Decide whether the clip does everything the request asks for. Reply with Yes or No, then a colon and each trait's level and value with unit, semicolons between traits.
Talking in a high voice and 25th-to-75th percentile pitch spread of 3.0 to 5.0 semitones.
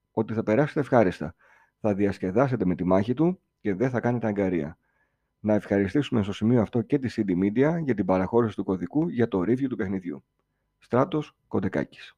No: low, 110 Hz; average, 4.4 semitones